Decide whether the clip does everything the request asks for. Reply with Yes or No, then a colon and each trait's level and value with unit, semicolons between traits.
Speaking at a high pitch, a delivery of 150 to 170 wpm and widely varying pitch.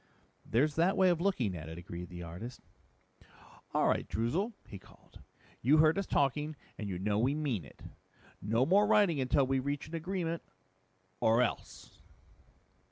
No: low, 135 Hz; average, 165 wpm; wide, 7.7 semitones